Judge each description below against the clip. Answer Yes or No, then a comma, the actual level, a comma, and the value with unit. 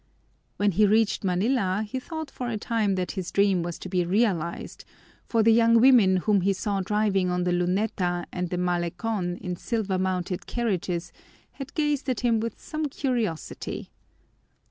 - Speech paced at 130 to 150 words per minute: No, average, 165 wpm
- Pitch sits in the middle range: No, high, 200 Hz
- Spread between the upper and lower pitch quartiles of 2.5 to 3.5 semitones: No, average, 4.2 semitones